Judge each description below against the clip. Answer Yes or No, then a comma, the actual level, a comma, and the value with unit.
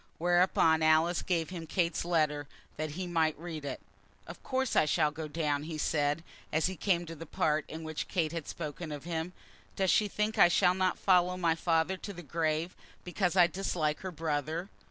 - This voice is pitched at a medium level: Yes, medium, 165 Hz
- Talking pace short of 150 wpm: No, average, 195 wpm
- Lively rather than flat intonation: No, narrow, 2.4 semitones